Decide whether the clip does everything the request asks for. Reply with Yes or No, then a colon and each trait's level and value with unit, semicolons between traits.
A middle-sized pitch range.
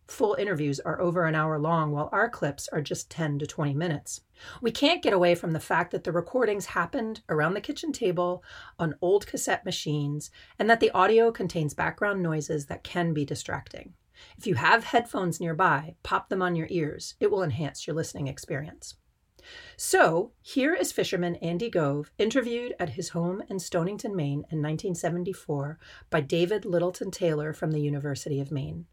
Yes: average, 4.8 semitones